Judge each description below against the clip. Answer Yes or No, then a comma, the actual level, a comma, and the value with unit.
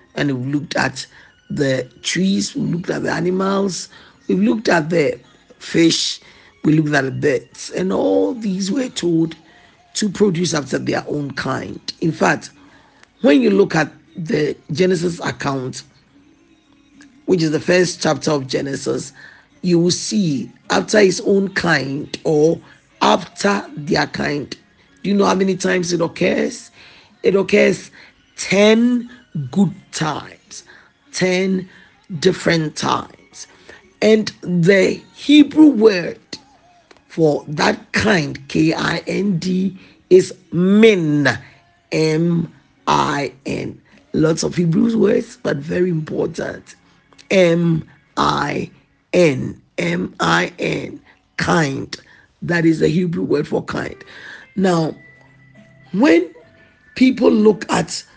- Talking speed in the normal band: No, slow, 110 wpm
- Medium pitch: Yes, medium, 180 Hz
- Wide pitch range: No, average, 4.6 semitones